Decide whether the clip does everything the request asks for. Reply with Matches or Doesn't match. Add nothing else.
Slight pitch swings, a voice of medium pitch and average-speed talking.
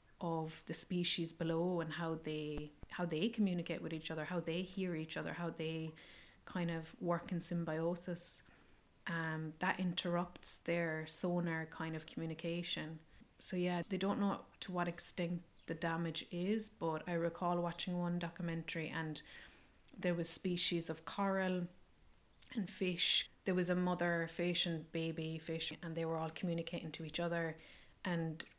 Matches